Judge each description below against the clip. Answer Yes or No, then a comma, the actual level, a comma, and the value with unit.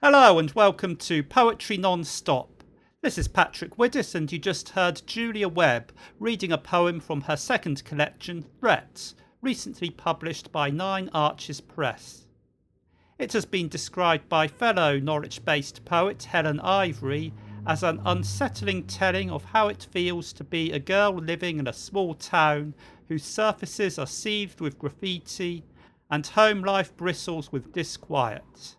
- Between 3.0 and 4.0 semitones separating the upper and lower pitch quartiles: No, average, 4.6 semitones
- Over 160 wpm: No, average, 145 wpm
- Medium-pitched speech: Yes, medium, 170 Hz